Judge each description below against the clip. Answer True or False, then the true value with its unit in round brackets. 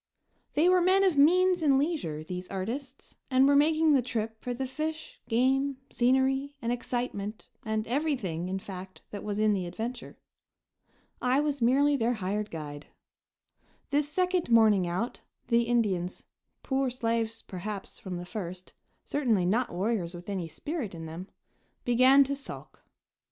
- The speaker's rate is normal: True (150 wpm)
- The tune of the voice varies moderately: False (6.3 semitones)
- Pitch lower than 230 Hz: False (235 Hz)